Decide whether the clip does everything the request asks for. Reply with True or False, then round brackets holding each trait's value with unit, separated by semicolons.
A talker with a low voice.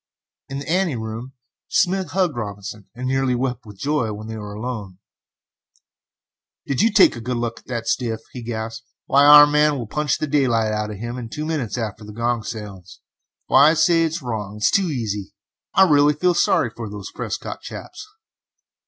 True (120 Hz)